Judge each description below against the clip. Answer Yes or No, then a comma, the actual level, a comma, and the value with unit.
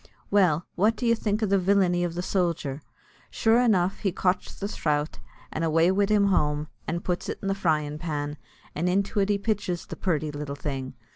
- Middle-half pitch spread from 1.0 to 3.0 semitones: No, average, 4.6 semitones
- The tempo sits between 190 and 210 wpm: Yes, average, 200 wpm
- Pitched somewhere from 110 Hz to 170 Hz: No, medium, 180 Hz